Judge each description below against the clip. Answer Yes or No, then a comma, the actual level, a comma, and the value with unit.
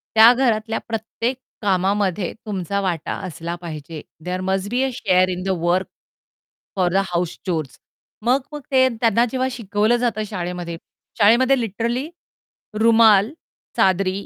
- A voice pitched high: Yes, high, 200 Hz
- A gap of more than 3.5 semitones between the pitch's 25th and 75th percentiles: Yes, average, 4.1 semitones